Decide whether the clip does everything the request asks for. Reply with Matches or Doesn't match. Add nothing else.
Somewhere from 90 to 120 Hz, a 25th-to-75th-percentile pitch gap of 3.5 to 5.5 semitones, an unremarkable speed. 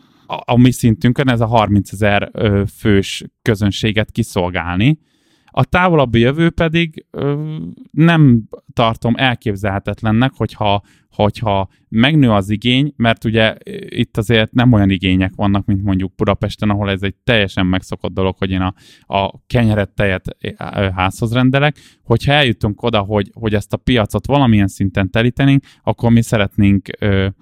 Matches